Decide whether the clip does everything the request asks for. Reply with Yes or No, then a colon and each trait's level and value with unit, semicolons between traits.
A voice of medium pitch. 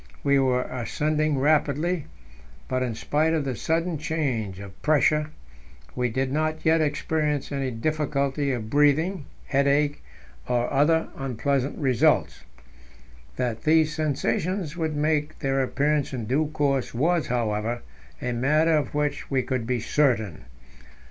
Yes: medium, 145 Hz